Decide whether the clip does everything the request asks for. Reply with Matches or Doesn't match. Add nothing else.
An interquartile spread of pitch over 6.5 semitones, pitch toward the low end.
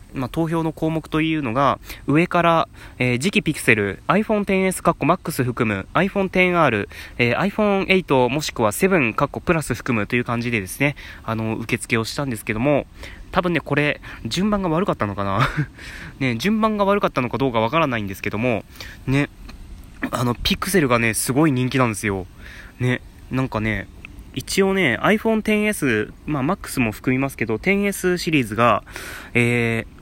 Matches